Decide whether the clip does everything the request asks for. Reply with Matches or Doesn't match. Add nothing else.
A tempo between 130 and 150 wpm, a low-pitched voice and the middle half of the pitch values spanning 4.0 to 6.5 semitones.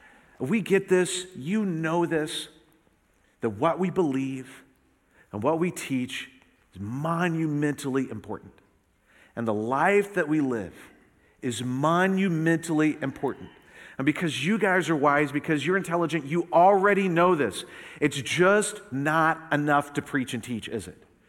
Doesn't match